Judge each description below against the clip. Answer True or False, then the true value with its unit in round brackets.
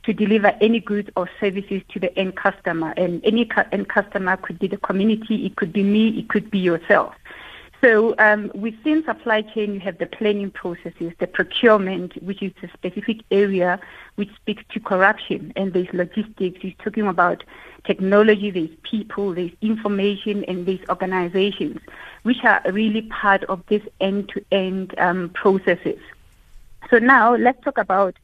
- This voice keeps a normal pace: True (165 wpm)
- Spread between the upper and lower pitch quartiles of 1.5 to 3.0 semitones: True (2.4 semitones)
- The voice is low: False (200 Hz)